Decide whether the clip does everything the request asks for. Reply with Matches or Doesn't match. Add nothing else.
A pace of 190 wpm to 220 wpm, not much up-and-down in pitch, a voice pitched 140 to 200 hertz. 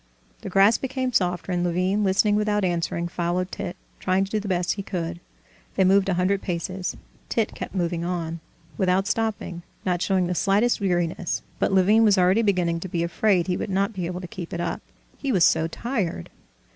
Matches